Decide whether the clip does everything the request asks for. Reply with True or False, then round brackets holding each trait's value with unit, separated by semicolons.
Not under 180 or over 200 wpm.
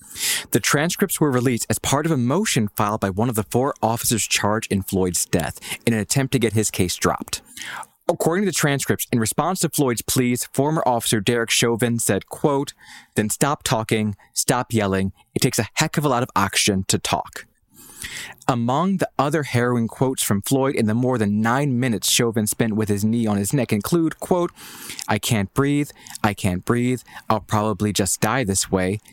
True (195 wpm)